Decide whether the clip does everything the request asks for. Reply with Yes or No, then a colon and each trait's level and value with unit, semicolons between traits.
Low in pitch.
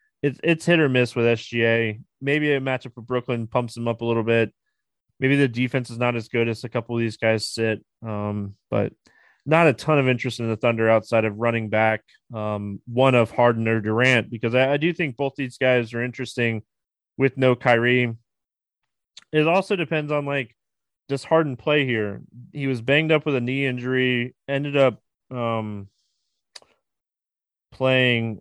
Yes: low, 125 Hz